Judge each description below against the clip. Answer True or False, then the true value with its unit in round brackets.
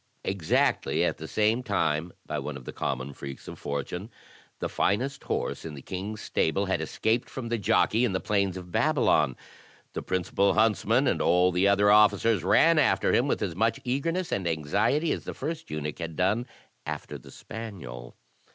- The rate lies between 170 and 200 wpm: True (180 wpm)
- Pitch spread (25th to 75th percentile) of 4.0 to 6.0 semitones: True (5.6 semitones)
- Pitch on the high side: False (100 Hz)